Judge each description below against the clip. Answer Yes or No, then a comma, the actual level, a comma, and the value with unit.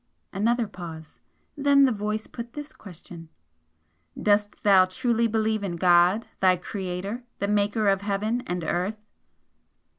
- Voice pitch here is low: No, high, 205 Hz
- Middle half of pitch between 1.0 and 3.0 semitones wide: No, average, 3.4 semitones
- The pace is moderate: No, slow, 130 wpm